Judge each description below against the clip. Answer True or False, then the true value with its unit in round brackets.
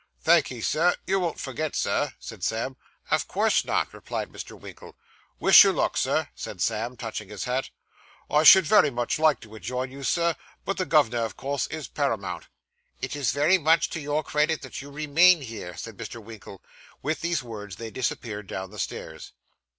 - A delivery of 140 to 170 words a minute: False (190 wpm)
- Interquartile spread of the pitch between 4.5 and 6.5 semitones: True (5.4 semitones)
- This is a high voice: False (135 Hz)